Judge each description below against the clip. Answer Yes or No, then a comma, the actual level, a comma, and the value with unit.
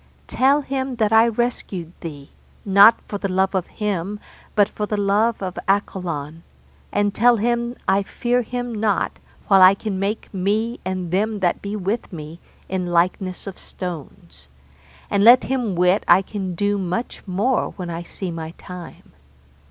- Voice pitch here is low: No, high, 200 Hz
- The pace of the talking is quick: No, average, 165 wpm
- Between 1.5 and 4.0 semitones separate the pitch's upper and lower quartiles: Yes, average, 3.5 semitones